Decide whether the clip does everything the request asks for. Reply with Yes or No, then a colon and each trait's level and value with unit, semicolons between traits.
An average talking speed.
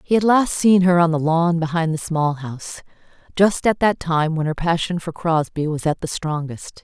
No: fast, 220 wpm